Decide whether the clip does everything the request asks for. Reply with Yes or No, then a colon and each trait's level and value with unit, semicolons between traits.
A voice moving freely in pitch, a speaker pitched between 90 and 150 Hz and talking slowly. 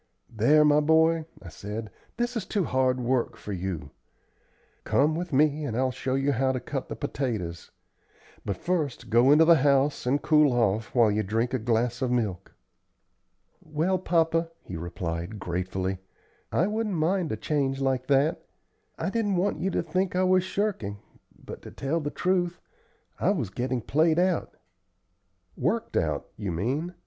No: wide, 6.5 semitones; medium, 140 Hz; average, 165 wpm